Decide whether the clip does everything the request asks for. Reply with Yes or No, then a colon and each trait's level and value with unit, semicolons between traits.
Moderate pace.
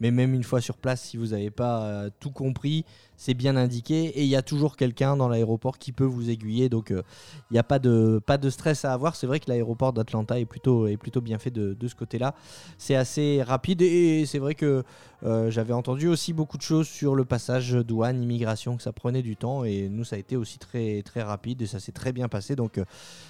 No: fast, 245 wpm